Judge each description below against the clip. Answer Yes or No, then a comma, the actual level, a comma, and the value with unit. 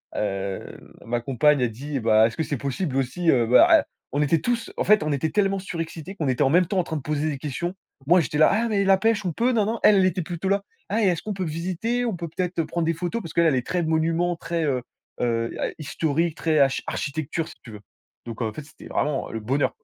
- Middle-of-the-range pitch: Yes, medium, 160 Hz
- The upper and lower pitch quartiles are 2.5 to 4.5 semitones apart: No, average, 5.1 semitones